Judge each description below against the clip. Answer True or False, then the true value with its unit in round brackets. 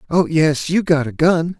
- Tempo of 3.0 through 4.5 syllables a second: True (4.4 syllables/s)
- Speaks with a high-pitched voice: False (160 Hz)